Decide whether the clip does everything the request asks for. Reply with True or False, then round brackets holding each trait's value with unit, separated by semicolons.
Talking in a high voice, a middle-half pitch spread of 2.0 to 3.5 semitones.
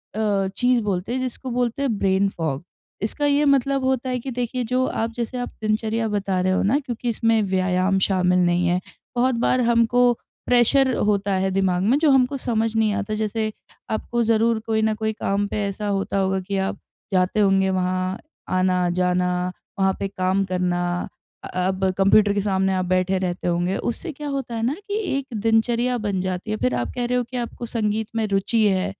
False (210 Hz; 4.1 semitones)